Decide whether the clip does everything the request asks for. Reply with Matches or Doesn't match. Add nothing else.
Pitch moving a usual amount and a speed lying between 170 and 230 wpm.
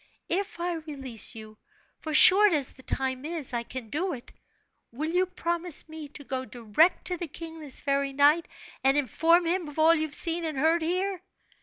Matches